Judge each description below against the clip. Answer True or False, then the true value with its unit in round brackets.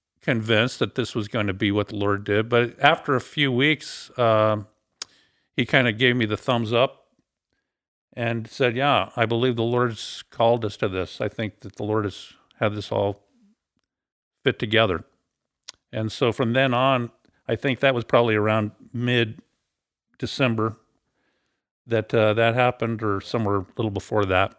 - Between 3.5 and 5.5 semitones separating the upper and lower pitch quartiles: False (2.8 semitones)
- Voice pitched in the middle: False (115 Hz)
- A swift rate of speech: False (170 wpm)